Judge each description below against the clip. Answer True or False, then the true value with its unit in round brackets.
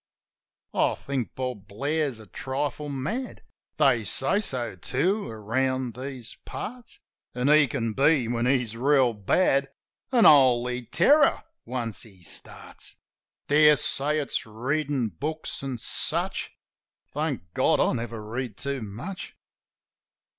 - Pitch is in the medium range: False (130 Hz)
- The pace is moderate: False (125 wpm)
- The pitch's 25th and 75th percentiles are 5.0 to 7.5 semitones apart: False (4.1 semitones)